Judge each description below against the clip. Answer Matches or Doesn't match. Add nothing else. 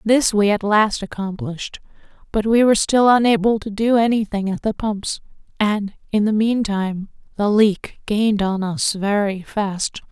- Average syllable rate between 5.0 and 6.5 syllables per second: Doesn't match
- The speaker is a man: Doesn't match